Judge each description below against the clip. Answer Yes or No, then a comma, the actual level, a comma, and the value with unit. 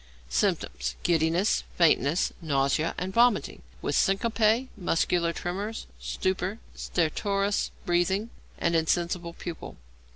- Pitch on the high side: No, medium, 180 Hz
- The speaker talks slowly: Yes, slow, 95 wpm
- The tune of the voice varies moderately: Yes, average, 3.2 semitones